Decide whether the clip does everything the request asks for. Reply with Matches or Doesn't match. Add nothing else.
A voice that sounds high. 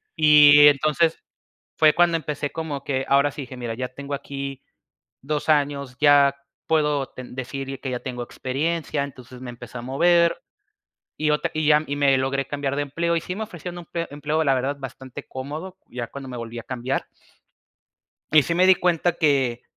Doesn't match